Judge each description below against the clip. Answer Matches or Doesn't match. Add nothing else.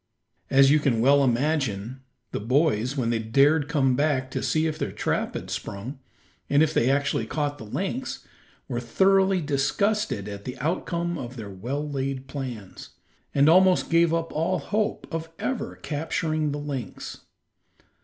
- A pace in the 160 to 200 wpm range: Matches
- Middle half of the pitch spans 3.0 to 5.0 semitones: Matches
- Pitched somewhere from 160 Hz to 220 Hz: Doesn't match